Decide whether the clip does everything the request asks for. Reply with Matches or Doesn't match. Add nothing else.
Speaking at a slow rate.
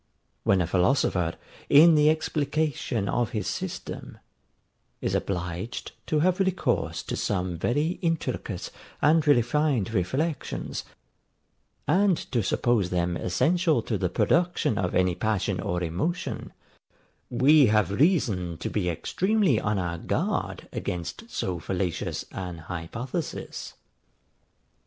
Matches